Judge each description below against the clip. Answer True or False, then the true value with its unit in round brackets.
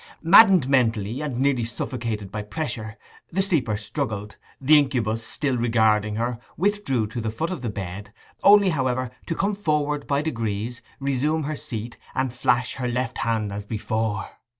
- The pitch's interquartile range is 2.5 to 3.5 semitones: False (5.0 semitones)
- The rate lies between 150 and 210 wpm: True (160 wpm)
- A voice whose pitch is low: True (125 Hz)